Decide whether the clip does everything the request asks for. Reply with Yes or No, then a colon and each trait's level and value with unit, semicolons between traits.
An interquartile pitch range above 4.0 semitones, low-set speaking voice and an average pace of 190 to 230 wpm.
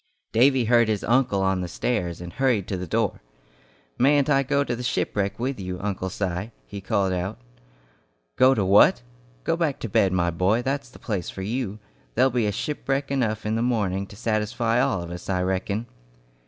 Yes: average, 4.9 semitones; low, 110 Hz; average, 195 wpm